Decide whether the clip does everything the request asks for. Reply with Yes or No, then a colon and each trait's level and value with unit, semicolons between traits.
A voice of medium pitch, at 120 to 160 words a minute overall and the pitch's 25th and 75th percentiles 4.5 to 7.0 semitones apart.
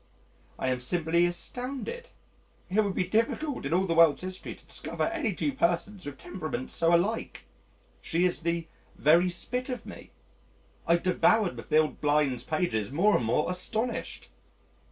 Yes: medium, 175 Hz; average, 155 wpm; wide, 5.5 semitones